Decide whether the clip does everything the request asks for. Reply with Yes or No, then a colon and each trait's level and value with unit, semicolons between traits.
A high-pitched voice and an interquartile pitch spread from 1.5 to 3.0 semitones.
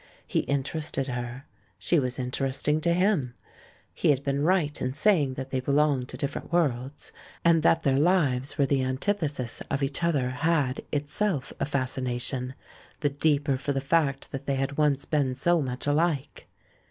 No: medium, 140 Hz; average, 2.7 semitones